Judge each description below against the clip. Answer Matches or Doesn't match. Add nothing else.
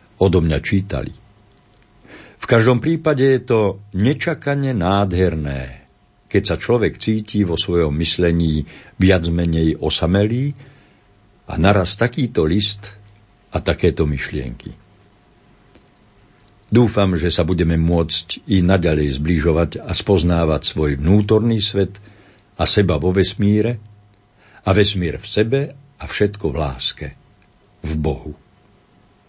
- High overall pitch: Doesn't match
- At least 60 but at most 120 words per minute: Matches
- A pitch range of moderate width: Matches